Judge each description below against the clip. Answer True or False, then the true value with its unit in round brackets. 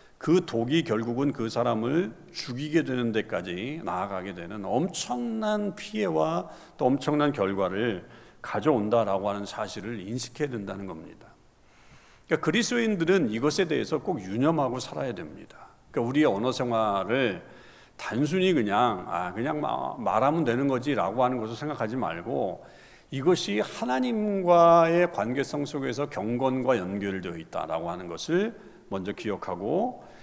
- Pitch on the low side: True (130 Hz)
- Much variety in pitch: True (6.9 semitones)